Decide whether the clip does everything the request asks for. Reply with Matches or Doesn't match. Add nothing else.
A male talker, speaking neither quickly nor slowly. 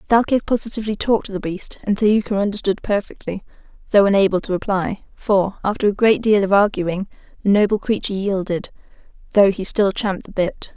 Doesn't match